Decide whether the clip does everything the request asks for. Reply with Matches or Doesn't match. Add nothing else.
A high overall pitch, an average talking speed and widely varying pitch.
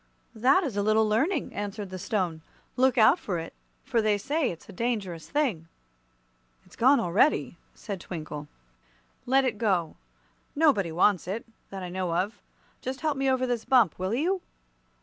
Matches